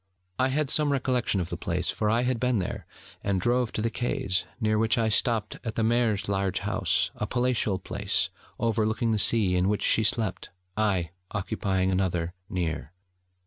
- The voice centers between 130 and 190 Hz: No, low, 110 Hz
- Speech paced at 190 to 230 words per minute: No, average, 180 wpm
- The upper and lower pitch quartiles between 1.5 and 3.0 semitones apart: No, average, 3.8 semitones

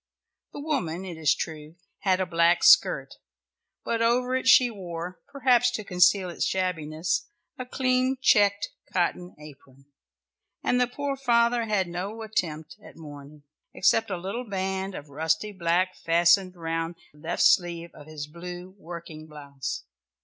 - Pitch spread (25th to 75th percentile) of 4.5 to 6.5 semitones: Yes, average, 5.2 semitones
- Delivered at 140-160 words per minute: Yes, average, 150 wpm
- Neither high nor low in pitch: Yes, medium, 180 Hz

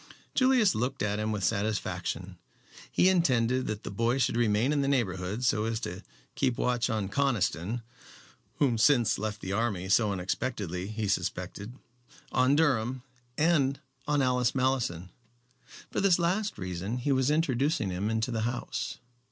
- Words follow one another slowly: No, average, 155 wpm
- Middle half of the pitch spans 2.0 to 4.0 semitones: No, average, 4.5 semitones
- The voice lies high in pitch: No, low, 120 Hz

